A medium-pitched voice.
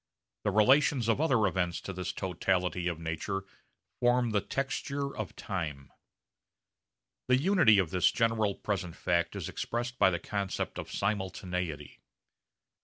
No: low, 100 Hz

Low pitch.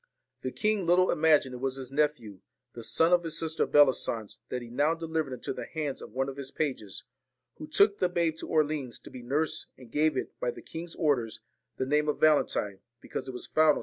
No: medium, 150 Hz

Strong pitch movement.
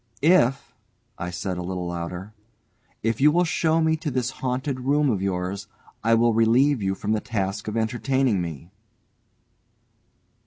Yes: wide, 5.8 semitones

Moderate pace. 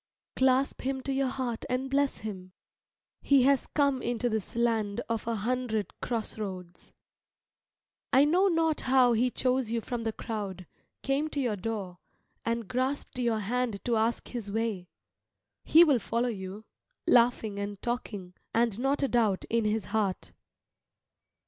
Yes: average, 155 wpm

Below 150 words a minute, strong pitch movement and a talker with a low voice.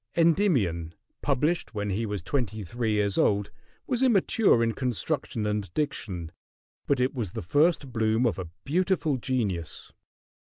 Yes: average, 140 wpm; wide, 6.4 semitones; low, 115 Hz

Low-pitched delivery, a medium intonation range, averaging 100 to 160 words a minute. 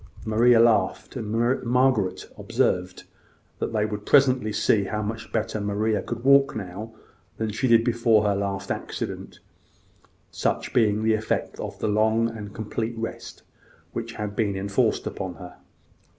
No: low, 110 Hz; narrow, 2.1 semitones; average, 150 wpm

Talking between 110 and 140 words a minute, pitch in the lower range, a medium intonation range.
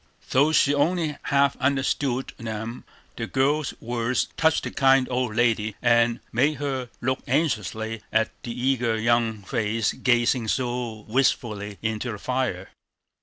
Yes: slow, 135 wpm; low, 120 Hz; average, 3.1 semitones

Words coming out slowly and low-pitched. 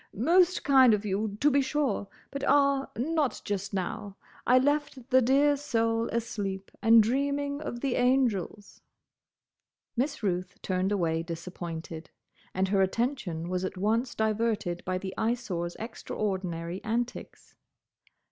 No: slow, 125 wpm; high, 220 Hz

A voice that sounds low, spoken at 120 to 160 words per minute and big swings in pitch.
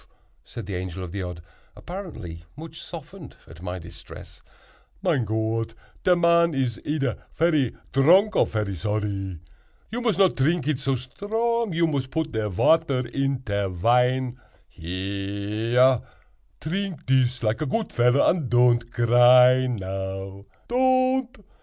Yes: low, 125 Hz; slow, 135 wpm; wide, 7.8 semitones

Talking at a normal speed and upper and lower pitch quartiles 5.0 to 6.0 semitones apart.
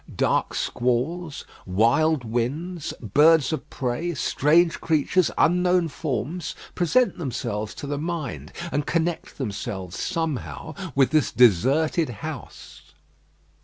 No: slow, 105 wpm; average, 5.3 semitones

